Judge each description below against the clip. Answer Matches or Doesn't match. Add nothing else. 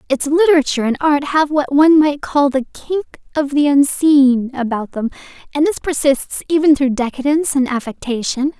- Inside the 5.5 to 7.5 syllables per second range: Doesn't match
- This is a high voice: Matches